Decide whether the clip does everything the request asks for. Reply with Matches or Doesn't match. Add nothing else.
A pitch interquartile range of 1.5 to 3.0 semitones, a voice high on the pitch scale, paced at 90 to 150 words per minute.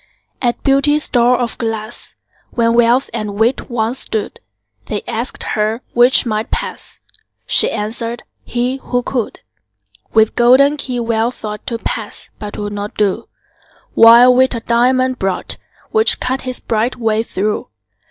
Matches